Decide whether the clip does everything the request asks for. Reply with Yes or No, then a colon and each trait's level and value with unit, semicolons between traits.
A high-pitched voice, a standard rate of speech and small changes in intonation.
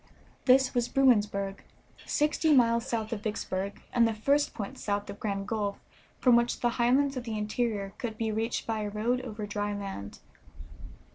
No: high, 220 Hz; average, 170 wpm; average, 3.0 semitones